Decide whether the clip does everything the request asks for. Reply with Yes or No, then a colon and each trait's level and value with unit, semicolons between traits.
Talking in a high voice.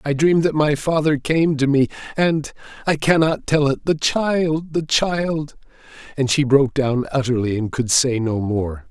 No: medium, 145 Hz